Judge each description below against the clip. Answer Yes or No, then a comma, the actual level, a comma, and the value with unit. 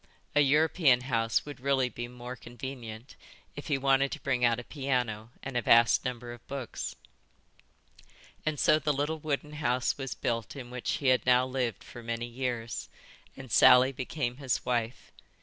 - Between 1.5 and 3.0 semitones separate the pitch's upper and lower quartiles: Yes, narrow, 2.4 semitones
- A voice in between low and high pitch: No, low, 125 Hz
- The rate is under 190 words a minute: Yes, average, 170 wpm